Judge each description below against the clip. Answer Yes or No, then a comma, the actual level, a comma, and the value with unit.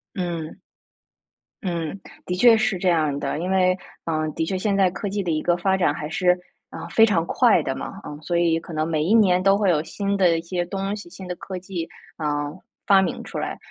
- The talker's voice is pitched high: No, medium, 180 Hz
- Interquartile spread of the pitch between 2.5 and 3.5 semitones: Yes, average, 3.1 semitones